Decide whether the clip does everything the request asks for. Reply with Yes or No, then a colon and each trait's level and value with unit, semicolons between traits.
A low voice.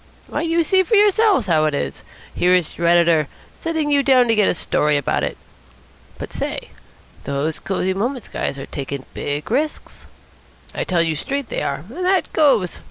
No: high, 195 Hz